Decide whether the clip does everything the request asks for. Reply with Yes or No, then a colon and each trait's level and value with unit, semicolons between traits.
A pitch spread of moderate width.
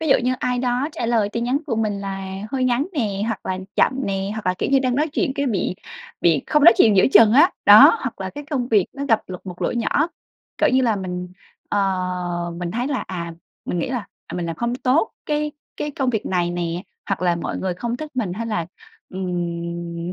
No: wide, 6.0 semitones